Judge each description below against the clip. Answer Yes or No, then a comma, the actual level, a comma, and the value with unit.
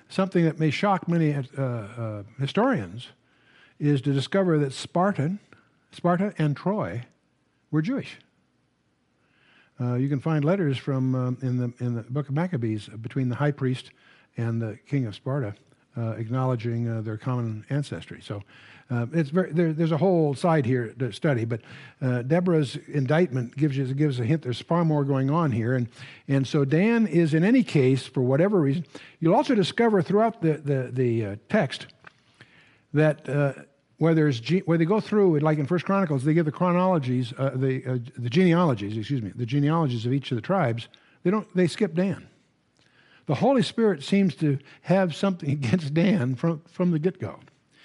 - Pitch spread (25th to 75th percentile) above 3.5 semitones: Yes, average, 5.2 semitones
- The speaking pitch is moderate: Yes, medium, 145 Hz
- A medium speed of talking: Yes, average, 180 wpm